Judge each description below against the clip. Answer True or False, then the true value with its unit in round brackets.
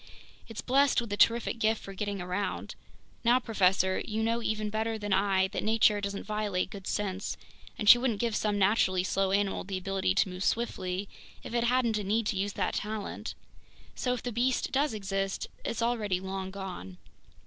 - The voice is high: True (205 Hz)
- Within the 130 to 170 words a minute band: False (190 wpm)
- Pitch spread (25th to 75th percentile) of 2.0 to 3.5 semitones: True (2.9 semitones)